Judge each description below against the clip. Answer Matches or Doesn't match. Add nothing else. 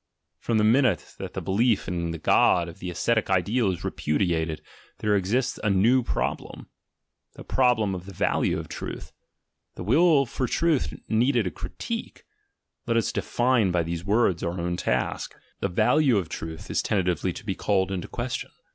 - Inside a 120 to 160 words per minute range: Doesn't match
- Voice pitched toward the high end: Doesn't match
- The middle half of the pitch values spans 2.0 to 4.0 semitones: Doesn't match